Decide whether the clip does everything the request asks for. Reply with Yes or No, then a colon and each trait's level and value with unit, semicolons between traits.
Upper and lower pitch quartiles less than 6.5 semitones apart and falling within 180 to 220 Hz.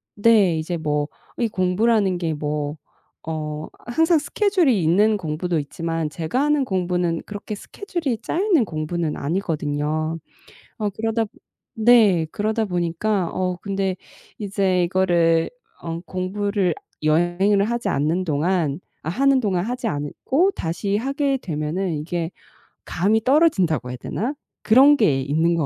Yes: average, 5.3 semitones; medium, 185 Hz